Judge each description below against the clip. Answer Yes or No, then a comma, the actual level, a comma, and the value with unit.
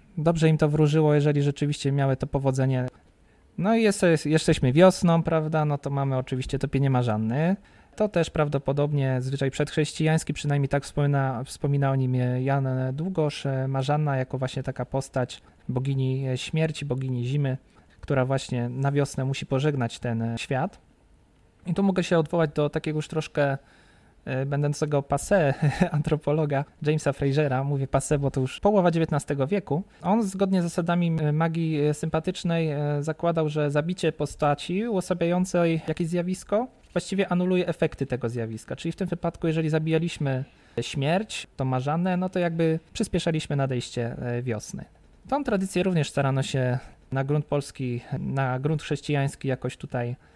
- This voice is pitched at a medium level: Yes, medium, 145 Hz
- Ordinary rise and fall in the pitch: Yes, average, 3.7 semitones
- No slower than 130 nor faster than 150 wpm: Yes, average, 140 wpm